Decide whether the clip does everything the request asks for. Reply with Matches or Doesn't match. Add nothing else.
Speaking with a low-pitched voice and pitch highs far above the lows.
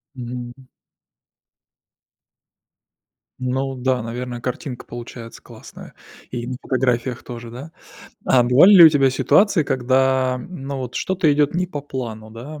Doesn't match